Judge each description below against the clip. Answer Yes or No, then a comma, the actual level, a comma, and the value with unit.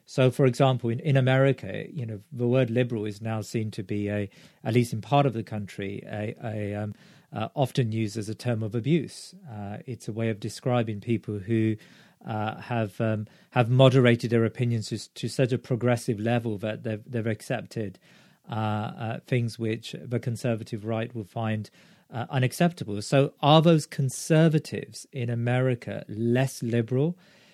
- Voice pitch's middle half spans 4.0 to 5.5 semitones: No, average, 3.2 semitones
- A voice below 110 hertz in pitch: No, low, 120 Hz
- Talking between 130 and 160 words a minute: No, average, 170 wpm